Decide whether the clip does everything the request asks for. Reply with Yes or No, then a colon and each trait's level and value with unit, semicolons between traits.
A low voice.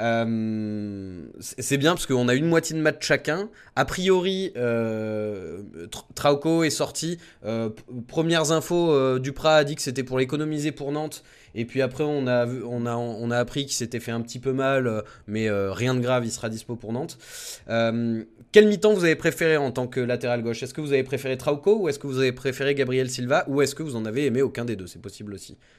Yes: low, 130 Hz